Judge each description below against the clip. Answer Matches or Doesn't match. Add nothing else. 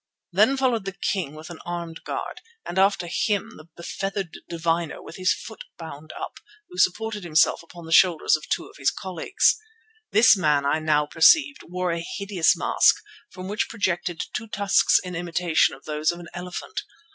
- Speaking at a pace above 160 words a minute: Matches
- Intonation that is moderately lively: Matches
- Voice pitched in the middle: Matches